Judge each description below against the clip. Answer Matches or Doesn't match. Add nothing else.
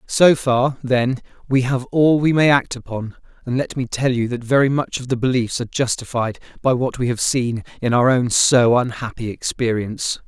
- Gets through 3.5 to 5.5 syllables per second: Matches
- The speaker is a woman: Doesn't match